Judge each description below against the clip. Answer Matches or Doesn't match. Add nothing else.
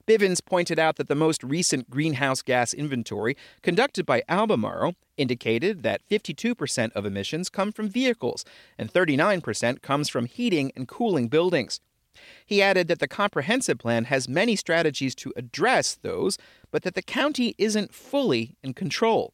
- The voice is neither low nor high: Matches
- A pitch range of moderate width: Doesn't match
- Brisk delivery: Doesn't match